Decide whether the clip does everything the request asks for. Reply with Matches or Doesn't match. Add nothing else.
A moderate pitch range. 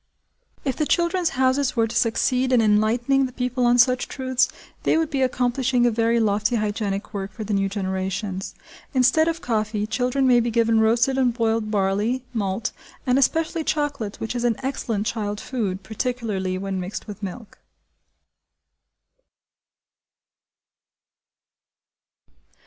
Matches